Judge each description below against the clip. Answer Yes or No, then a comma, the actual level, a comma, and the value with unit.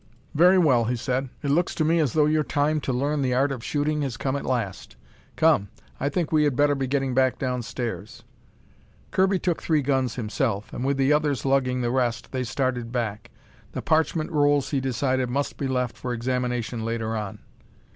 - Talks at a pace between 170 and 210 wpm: Yes, average, 195 wpm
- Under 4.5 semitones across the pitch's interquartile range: Yes, average, 3.0 semitones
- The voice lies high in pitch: No, low, 130 Hz